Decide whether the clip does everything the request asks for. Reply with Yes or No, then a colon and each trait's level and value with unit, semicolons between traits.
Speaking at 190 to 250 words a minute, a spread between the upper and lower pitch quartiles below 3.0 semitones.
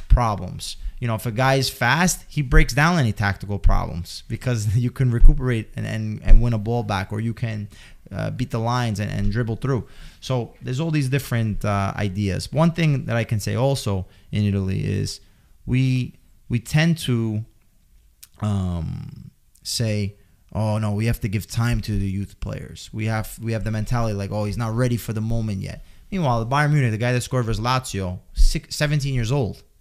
No: average, 200 wpm; average, 3.6 semitones